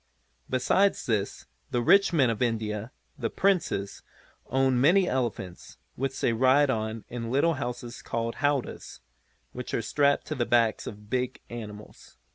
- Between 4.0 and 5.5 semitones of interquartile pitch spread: No, average, 3.2 semitones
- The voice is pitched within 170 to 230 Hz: No, low, 120 Hz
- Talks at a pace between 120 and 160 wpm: Yes, average, 150 wpm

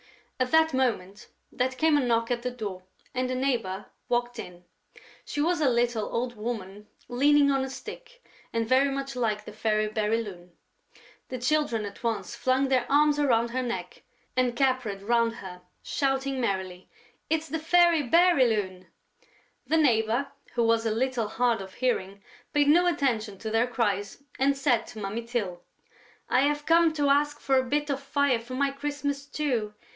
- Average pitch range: Yes, average, 4.3 semitones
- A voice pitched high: Yes, very high, 250 Hz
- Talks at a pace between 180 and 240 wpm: No, average, 170 wpm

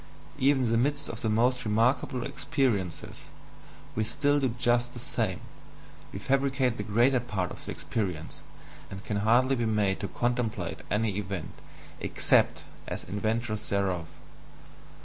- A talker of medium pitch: No, low, 115 Hz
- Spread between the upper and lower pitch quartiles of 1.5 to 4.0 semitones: Yes, average, 3.7 semitones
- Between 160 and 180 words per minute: No, average, 145 wpm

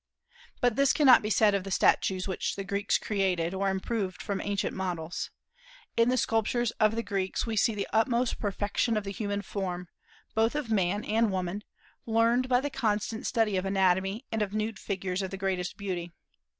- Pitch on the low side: No, high, 205 Hz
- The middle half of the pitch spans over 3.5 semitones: No, average, 2.9 semitones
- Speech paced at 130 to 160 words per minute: No, average, 190 wpm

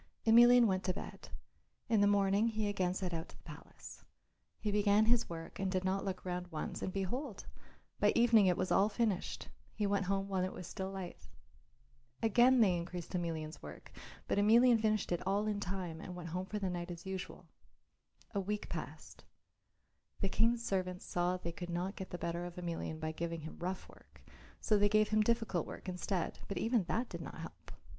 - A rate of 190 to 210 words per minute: Yes, average, 200 wpm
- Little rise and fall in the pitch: No, average, 3.1 semitones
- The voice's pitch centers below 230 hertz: Yes, high, 190 Hz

